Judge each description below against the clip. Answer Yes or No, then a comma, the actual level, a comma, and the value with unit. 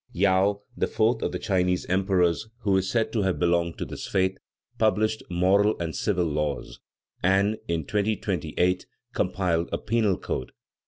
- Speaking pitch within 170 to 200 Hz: No, very low, 95 Hz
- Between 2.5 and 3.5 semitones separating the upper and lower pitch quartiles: Yes, average, 2.8 semitones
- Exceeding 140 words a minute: Yes, average, 155 wpm